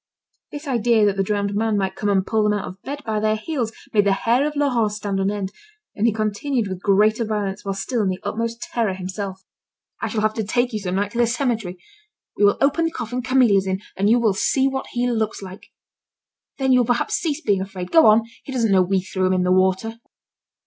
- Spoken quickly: Yes, fast, 240 wpm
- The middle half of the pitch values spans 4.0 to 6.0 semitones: No, average, 3.6 semitones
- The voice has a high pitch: Yes, high, 215 Hz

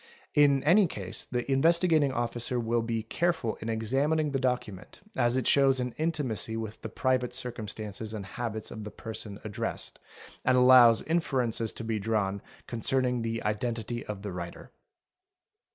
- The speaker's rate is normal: Yes, average, 155 wpm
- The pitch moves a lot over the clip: No, average, 3.4 semitones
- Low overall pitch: Yes, low, 120 Hz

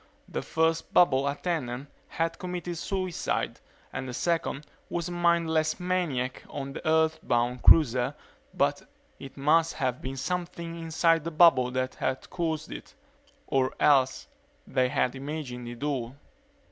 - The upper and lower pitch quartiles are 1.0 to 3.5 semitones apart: No, average, 4.3 semitones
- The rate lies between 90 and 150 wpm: Yes, slow, 135 wpm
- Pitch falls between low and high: Yes, medium, 155 Hz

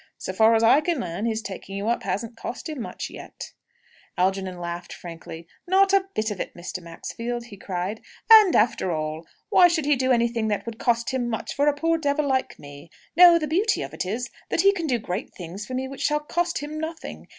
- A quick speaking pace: Yes, fast, 225 wpm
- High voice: Yes, high, 235 Hz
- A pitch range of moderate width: No, wide, 7.8 semitones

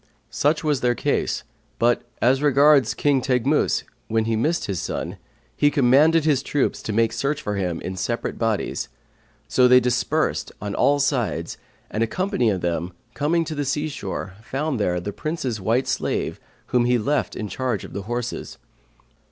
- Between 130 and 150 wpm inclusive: No, average, 175 wpm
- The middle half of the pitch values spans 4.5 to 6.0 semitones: Yes, average, 5.0 semitones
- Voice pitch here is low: Yes, low, 125 Hz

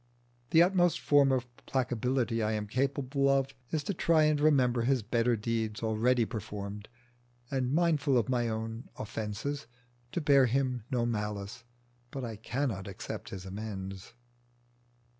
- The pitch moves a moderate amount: Yes, average, 4.1 semitones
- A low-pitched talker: Yes, low, 120 Hz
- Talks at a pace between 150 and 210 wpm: No, average, 140 wpm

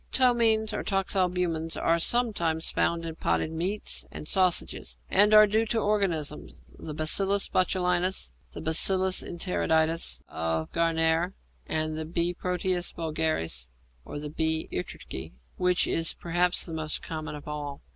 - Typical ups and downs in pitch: Yes, average, 3.1 semitones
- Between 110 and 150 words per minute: Yes, slow, 135 wpm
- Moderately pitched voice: Yes, medium, 165 Hz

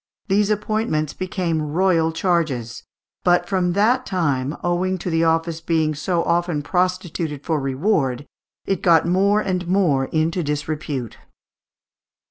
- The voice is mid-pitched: Yes, medium, 170 Hz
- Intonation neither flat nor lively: Yes, average, 3.4 semitones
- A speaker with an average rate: No, slow, 125 wpm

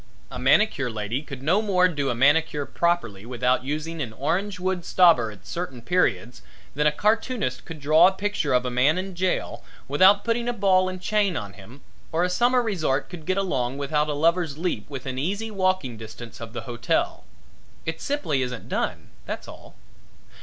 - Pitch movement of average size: No, wide, 6.6 semitones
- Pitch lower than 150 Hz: No, medium, 155 Hz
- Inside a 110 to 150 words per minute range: No, average, 185 wpm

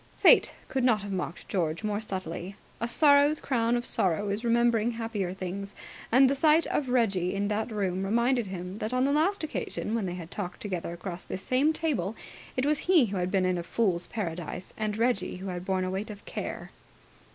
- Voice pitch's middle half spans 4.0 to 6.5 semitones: Yes, average, 4.7 semitones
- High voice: Yes, high, 210 Hz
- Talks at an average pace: No, fast, 210 wpm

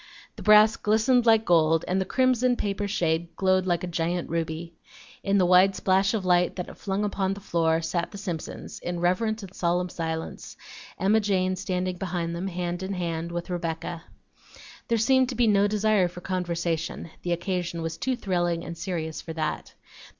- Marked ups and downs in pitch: No, average, 2.9 semitones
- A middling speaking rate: Yes, average, 185 wpm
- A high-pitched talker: No, medium, 180 Hz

